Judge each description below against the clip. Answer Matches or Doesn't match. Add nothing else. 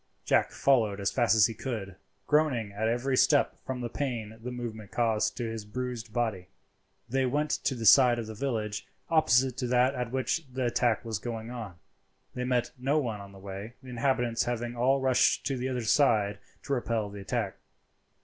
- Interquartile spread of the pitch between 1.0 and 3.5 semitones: Matches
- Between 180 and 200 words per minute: Matches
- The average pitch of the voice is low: Matches